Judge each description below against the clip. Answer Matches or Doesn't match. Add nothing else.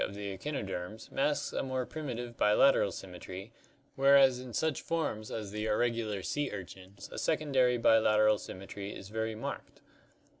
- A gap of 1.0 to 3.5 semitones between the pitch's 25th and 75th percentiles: Doesn't match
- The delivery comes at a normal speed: Matches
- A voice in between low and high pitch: Doesn't match